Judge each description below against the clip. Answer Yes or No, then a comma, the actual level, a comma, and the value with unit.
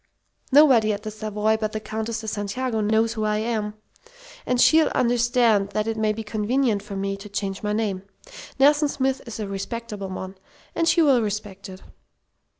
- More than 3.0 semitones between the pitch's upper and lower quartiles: No, narrow, 2.4 semitones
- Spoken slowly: No, average, 175 wpm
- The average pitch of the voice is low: No, high, 215 Hz